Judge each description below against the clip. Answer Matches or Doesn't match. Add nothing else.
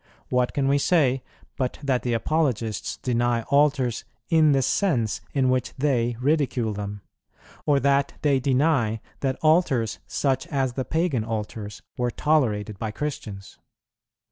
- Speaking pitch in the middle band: Doesn't match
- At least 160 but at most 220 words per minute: Doesn't match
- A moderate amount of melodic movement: Matches